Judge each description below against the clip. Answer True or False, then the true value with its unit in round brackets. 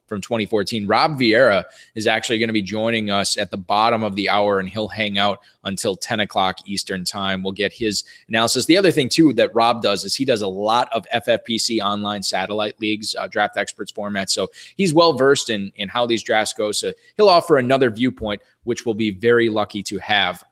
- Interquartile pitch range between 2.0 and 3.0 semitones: True (2.6 semitones)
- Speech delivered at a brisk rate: True (215 wpm)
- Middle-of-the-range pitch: False (110 Hz)